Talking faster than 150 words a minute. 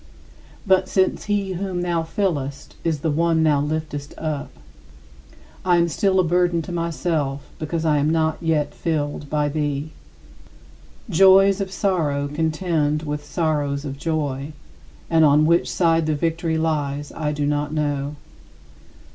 No: average, 145 wpm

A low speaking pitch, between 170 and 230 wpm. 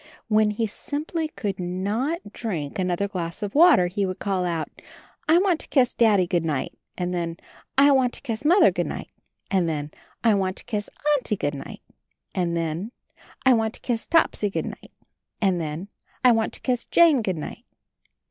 No: high, 205 Hz; average, 200 wpm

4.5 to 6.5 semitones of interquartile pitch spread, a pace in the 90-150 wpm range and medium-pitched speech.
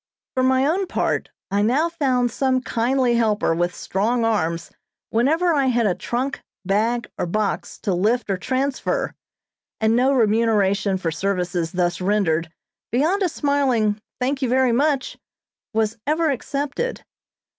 No: average, 4.9 semitones; average, 145 wpm; high, 235 Hz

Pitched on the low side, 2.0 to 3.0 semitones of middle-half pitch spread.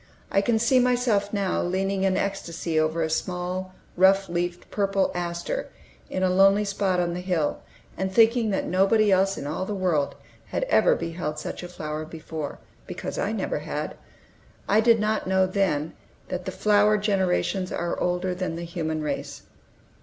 No: medium, 185 Hz; narrow, 2.6 semitones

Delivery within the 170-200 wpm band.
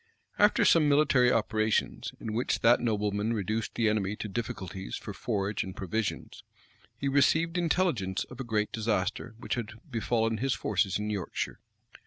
No: average, 160 wpm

